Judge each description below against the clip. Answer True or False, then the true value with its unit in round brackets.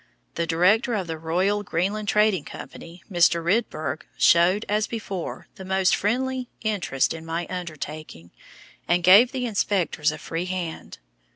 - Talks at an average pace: True (145 wpm)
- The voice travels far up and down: False (4.2 semitones)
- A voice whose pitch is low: False (185 Hz)